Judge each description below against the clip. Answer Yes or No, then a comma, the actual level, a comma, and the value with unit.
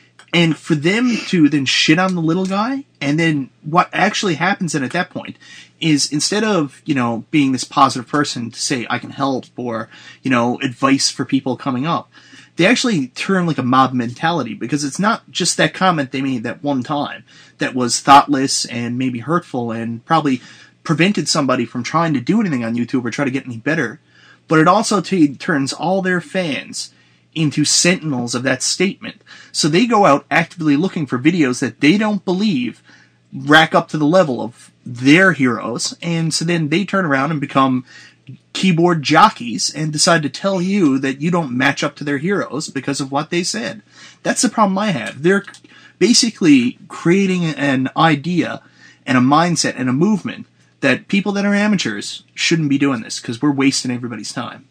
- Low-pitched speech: No, medium, 155 Hz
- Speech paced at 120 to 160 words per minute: No, average, 190 wpm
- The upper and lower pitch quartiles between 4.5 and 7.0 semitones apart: Yes, wide, 5.5 semitones